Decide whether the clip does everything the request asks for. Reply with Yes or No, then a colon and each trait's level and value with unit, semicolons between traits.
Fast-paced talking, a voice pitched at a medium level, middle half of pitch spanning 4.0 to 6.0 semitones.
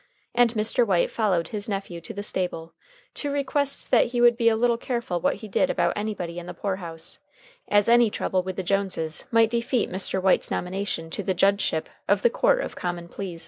No: fast, 210 wpm; high, 200 Hz; average, 4.8 semitones